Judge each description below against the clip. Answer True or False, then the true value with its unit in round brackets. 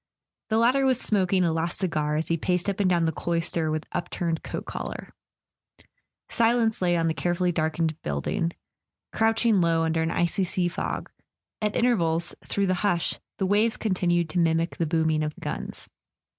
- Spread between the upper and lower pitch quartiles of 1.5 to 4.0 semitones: True (3.4 semitones)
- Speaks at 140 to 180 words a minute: True (175 wpm)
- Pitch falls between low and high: True (175 Hz)